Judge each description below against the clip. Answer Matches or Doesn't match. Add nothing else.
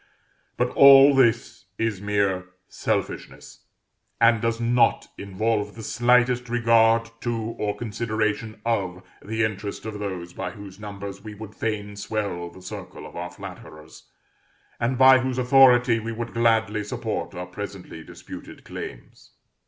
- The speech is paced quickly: Doesn't match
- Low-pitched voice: Matches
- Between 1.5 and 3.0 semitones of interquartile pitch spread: Matches